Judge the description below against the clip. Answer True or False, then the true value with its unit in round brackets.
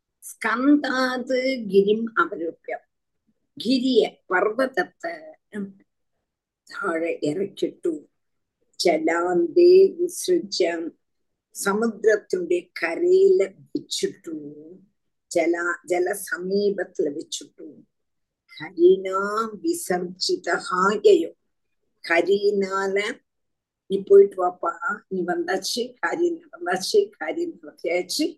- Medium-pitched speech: False (245 Hz)